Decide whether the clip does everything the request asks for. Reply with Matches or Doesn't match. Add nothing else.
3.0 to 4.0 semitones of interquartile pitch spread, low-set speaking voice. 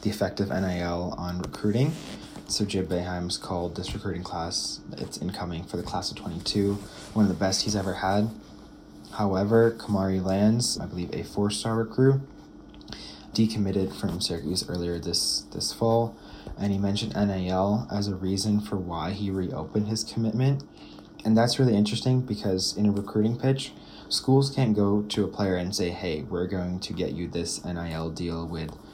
Matches